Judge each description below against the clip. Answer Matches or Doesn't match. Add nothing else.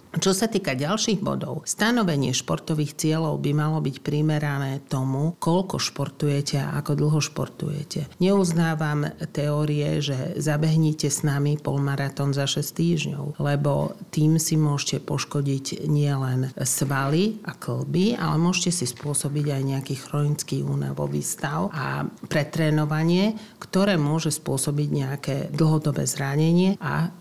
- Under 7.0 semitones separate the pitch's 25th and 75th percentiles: Matches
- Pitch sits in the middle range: Matches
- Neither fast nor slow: Matches